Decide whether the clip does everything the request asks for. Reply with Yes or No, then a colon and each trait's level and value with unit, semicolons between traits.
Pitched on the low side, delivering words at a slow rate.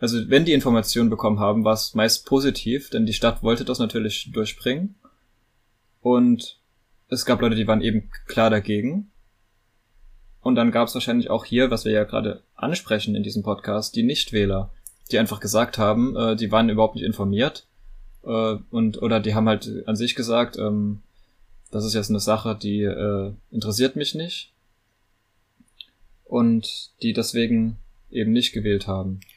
No: low, 110 Hz; average, 165 wpm